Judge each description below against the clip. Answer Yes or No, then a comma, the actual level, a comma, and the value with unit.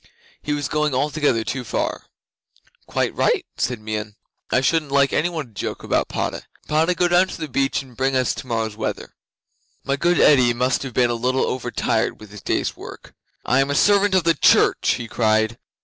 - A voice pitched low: Yes, low, 130 Hz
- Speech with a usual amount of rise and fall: Yes, average, 4.5 semitones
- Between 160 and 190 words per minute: No, average, 200 wpm